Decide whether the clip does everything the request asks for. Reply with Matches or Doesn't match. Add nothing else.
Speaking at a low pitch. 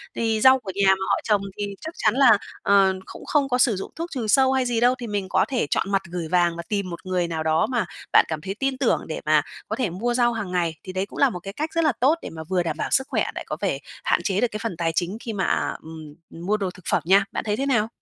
Doesn't match